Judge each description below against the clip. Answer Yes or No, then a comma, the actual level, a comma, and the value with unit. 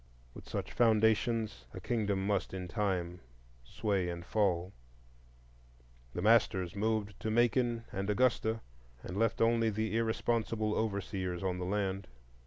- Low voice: Yes, low, 105 Hz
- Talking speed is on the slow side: Yes, slow, 130 wpm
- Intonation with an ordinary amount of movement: Yes, average, 3.1 semitones